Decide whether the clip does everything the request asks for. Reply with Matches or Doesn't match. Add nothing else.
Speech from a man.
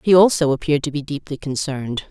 Doesn't match